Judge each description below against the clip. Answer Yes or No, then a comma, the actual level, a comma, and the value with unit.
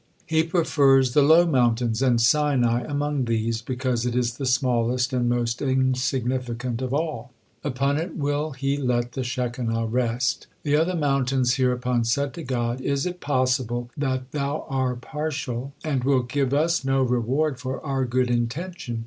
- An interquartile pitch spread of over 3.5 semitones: No, average, 2.7 semitones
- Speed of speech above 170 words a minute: No, average, 160 wpm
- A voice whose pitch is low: Yes, low, 130 Hz